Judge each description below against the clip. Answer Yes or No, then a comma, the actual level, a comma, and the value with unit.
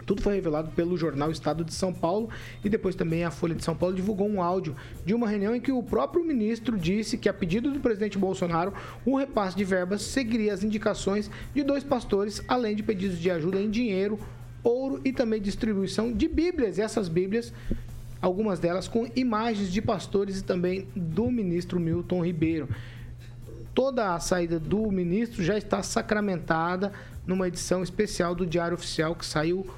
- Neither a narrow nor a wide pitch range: Yes, average, 4.2 semitones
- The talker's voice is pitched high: Yes, high, 195 Hz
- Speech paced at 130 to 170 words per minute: No, average, 180 wpm